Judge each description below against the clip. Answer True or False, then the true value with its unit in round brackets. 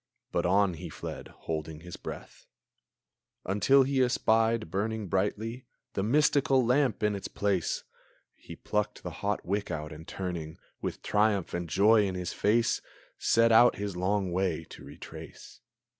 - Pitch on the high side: False (100 Hz)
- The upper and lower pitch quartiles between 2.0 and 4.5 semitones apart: True (4.0 semitones)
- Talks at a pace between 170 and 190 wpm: False (150 wpm)